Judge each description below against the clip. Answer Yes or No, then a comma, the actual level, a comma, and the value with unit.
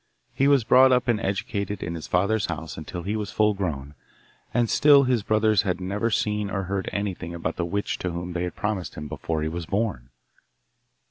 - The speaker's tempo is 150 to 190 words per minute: No, fast, 205 wpm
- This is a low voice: Yes, low, 100 Hz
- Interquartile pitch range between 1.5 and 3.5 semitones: No, average, 3.9 semitones